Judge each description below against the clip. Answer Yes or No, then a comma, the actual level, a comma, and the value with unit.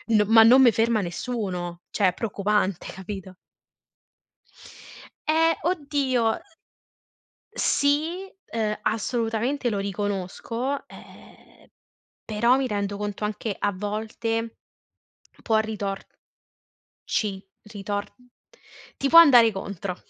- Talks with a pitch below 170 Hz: No, high, 220 Hz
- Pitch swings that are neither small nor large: Yes, average, 3.6 semitones